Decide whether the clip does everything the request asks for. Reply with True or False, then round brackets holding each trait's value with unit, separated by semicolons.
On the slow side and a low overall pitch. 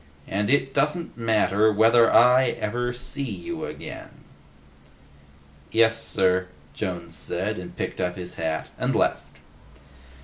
True (125 wpm; 105 Hz)